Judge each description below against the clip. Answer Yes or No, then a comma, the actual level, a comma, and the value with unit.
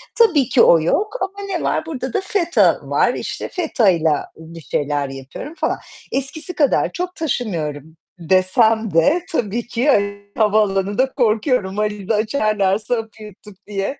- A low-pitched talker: No, high, 220 Hz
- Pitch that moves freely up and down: Yes, wide, 7.0 semitones